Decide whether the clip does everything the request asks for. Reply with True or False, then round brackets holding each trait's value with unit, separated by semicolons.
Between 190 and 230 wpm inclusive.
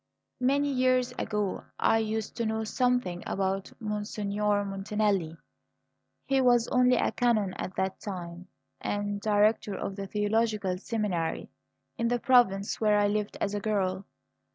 False (140 wpm)